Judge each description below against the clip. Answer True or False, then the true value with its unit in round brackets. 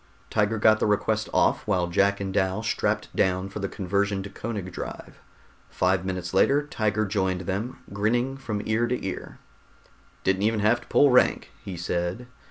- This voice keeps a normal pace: True (175 wpm)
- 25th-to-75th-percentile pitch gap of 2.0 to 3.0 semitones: True (2.6 semitones)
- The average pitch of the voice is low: True (100 Hz)